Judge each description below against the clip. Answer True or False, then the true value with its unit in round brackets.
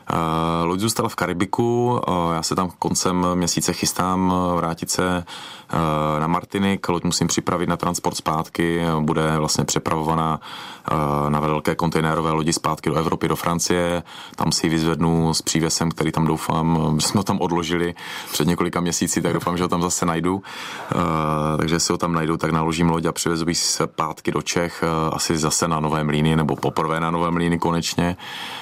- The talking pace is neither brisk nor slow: False (180 wpm)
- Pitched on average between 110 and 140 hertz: False (85 Hz)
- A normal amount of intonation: False (1.7 semitones)